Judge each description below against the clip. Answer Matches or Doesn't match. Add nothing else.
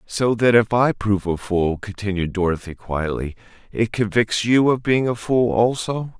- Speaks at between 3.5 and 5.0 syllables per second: Matches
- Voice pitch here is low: Matches